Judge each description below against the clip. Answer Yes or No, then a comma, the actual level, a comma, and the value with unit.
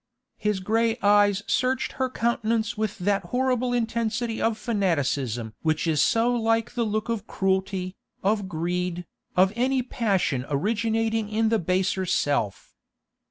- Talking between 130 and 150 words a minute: Yes, slow, 135 wpm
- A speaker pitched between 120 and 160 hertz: No, high, 210 Hz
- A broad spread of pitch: No, average, 3.9 semitones